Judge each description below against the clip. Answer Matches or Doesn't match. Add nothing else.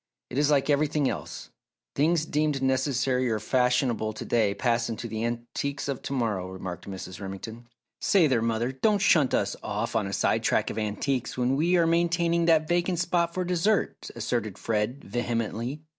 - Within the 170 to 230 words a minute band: Matches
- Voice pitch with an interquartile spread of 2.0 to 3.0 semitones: Doesn't match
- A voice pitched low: Matches